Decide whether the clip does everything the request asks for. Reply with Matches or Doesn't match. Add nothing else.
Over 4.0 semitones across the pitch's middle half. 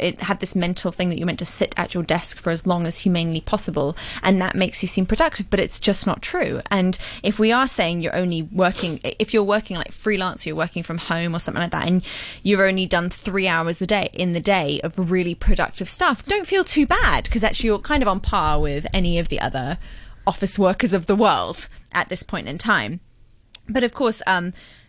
Doesn't match